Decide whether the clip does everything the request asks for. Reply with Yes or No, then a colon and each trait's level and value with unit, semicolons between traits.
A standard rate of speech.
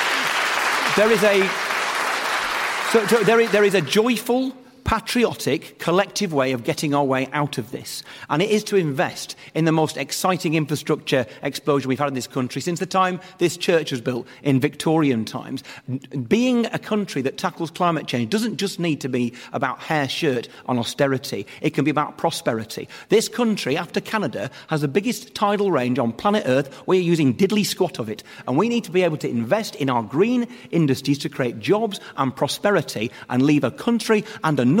Yes: average, 190 wpm